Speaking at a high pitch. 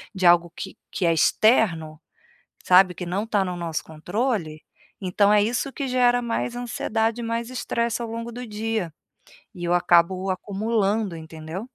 Yes: high, 205 Hz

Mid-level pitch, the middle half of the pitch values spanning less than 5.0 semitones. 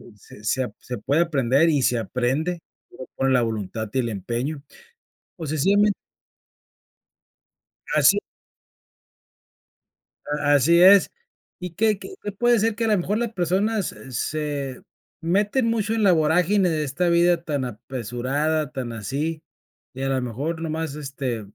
No: medium, 155 Hz; wide, 5.6 semitones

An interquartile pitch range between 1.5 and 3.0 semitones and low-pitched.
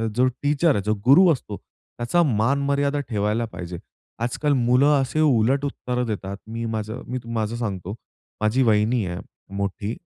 No: average, 4.4 semitones; low, 120 Hz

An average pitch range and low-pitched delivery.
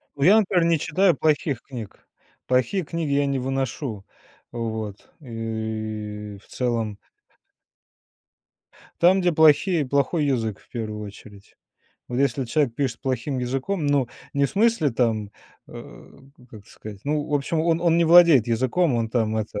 No: wide, 5.8 semitones; low, 130 Hz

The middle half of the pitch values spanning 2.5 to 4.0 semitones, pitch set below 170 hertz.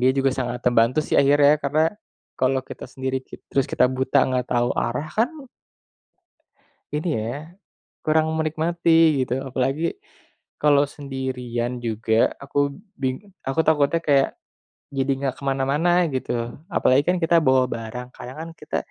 Yes: average, 3.5 semitones; low, 135 Hz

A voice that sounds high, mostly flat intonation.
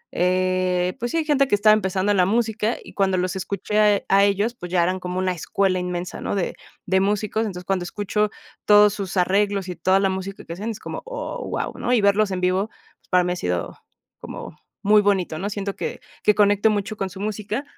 Yes: high, 195 Hz; narrow, 2.3 semitones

